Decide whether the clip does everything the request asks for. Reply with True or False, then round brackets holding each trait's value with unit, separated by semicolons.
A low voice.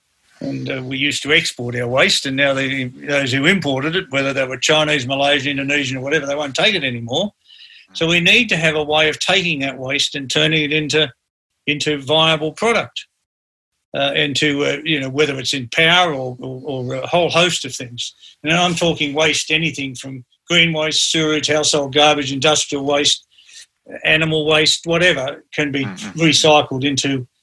False (145 Hz)